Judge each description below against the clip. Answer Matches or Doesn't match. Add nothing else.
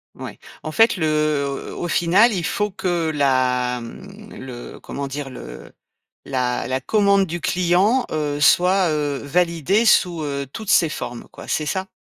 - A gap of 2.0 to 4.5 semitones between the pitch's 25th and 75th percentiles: Doesn't match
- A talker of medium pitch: Matches